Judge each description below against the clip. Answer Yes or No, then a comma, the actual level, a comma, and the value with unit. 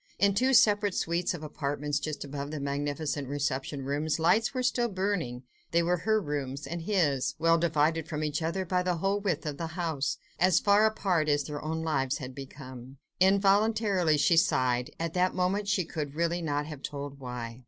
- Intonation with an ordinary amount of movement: Yes, average, 4.4 semitones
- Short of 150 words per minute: No, average, 185 wpm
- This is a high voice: No, medium, 160 Hz